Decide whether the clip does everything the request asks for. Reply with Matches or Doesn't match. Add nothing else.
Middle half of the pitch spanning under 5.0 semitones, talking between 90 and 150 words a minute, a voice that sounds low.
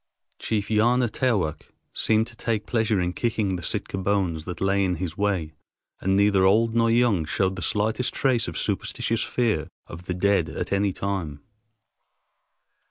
Doesn't match